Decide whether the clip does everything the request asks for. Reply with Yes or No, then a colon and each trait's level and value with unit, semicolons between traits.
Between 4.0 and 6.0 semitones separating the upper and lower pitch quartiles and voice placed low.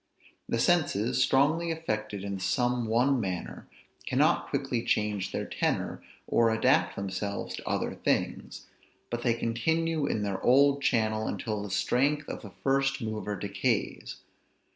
Yes: average, 4.7 semitones; low, 115 Hz